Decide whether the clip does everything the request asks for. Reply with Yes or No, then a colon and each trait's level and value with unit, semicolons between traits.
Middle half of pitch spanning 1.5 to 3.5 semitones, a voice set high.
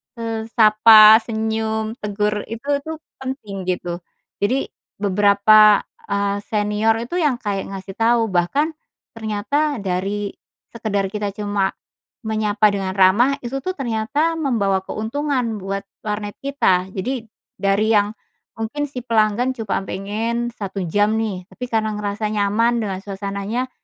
Yes: average, 2.8 semitones; high, 215 Hz